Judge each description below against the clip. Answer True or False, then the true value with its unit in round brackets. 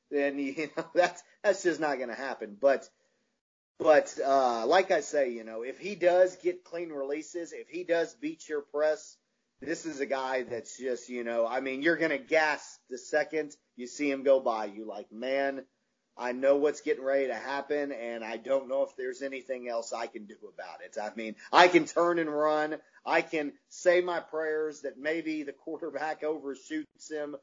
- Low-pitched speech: False (150 Hz)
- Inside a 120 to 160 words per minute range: False (195 wpm)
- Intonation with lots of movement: False (3.7 semitones)